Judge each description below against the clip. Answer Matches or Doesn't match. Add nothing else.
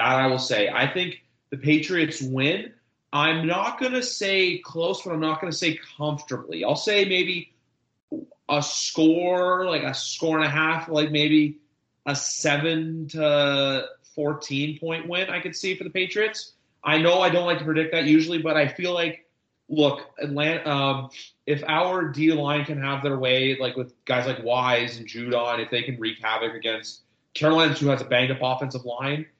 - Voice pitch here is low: Doesn't match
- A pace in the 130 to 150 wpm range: Doesn't match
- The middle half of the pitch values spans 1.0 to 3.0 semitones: Doesn't match